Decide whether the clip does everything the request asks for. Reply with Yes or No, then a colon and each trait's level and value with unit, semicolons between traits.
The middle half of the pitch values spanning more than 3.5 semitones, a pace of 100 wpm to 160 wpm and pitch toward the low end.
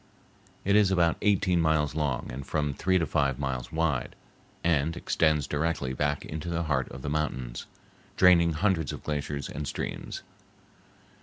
No: average, 3.1 semitones; average, 155 wpm; very low, 75 Hz